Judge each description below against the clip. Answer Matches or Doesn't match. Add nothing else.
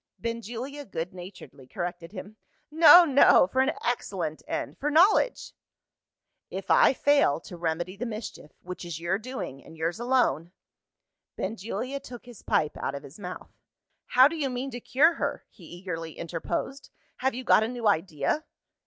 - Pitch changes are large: Matches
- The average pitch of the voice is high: Matches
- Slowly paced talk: Doesn't match